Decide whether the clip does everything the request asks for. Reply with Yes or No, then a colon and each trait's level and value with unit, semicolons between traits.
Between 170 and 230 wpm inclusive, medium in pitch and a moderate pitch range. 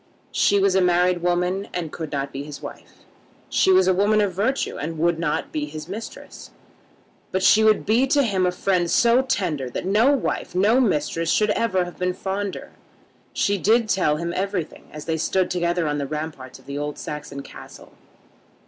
Yes: average, 195 wpm; medium, 180 Hz; average, 4.6 semitones